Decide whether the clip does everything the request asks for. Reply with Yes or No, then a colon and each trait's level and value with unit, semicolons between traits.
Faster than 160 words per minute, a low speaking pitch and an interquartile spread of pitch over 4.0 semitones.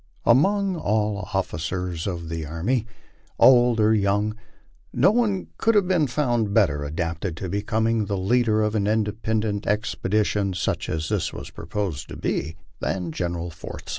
No: average, 155 wpm; low, 105 Hz; average, 4.5 semitones